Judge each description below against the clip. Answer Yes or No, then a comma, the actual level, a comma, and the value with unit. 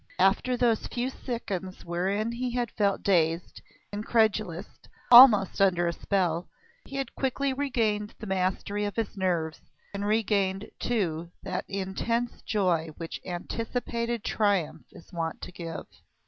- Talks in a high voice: Yes, high, 200 Hz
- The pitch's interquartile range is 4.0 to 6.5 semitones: Yes, average, 4.3 semitones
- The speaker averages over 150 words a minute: No, slow, 135 wpm